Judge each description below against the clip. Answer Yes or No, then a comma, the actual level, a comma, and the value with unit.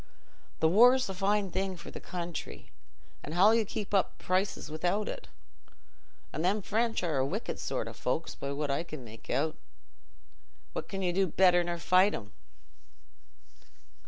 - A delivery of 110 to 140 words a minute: No, average, 165 wpm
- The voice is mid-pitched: Yes, medium, 180 Hz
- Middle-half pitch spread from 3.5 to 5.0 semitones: Yes, average, 4.0 semitones